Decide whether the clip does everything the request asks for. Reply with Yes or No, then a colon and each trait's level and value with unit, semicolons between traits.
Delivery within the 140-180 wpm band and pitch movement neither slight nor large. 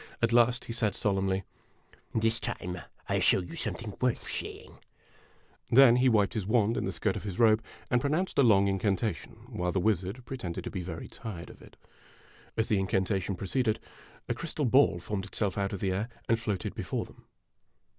No: average, 200 wpm; average, 3.5 semitones